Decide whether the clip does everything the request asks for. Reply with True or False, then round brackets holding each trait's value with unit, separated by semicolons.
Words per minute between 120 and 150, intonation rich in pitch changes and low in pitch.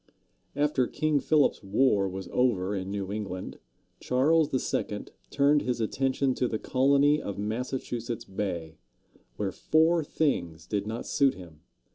True (135 wpm; 6.2 semitones; 120 Hz)